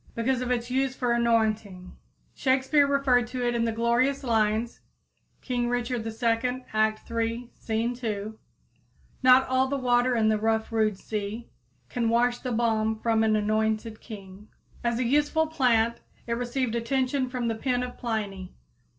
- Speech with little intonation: Yes, narrow, 2.3 semitones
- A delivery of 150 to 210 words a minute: Yes, average, 160 wpm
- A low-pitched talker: No, high, 235 Hz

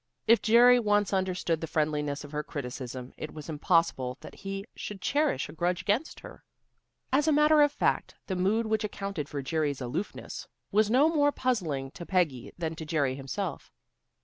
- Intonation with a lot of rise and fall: Yes, wide, 6.7 semitones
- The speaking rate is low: No, average, 175 wpm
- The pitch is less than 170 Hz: No, medium, 180 Hz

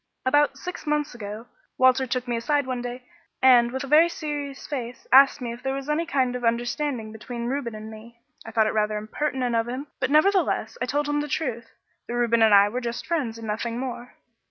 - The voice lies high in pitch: Yes, very high, 250 Hz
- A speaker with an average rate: No, fast, 220 wpm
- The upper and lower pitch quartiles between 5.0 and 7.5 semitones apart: No, average, 3.5 semitones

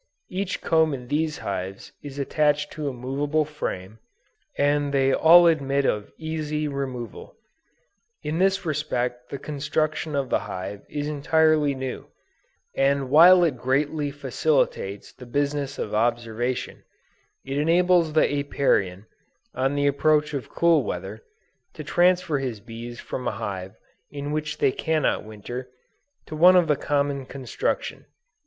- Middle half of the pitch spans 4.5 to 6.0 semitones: No, average, 3.4 semitones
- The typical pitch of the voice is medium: Yes, medium, 145 Hz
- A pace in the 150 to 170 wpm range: No, average, 140 wpm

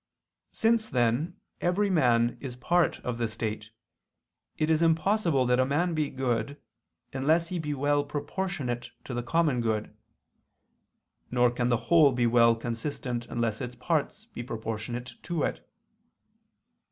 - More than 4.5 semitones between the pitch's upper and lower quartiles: Yes, average, 5.2 semitones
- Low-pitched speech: Yes, low, 130 Hz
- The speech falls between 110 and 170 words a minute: Yes, average, 145 wpm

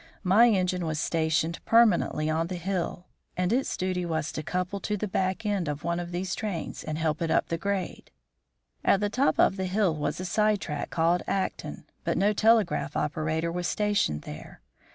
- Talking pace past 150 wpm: Yes, average, 195 wpm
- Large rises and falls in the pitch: No, average, 3.7 semitones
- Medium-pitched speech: Yes, medium, 180 Hz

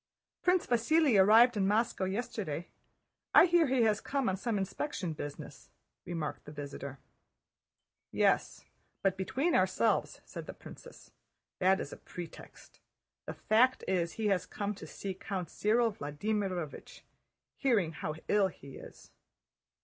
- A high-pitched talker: Yes, high, 200 Hz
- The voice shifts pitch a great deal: No, average, 4.9 semitones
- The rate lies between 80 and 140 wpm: Yes, slow, 135 wpm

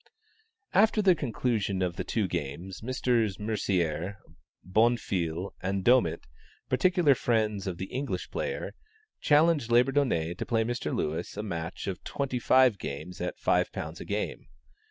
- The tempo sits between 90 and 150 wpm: Yes, slow, 135 wpm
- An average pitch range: No, wide, 5.8 semitones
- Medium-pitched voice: No, low, 110 Hz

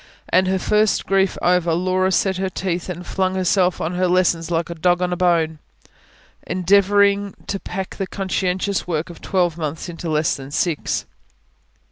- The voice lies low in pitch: No, medium, 180 Hz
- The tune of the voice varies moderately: No, narrow, 1.8 semitones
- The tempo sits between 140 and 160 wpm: No, average, 170 wpm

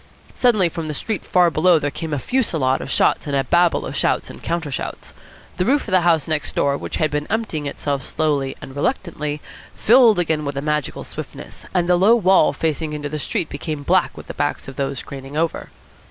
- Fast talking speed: Yes, fast, 215 wpm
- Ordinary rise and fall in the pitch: Yes, average, 3.6 semitones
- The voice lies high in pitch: No, medium, 155 Hz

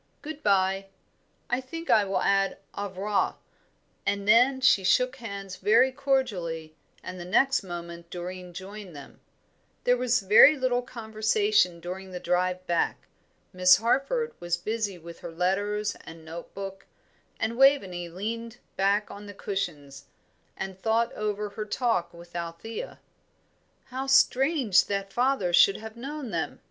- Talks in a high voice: Yes, high, 200 Hz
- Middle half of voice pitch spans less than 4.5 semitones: No, average, 5.0 semitones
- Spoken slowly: No, average, 145 wpm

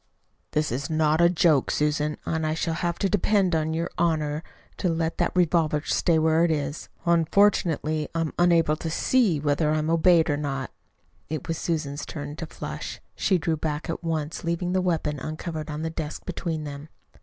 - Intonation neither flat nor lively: No, narrow, 2.0 semitones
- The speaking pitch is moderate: Yes, medium, 160 Hz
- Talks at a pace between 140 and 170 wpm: No, average, 190 wpm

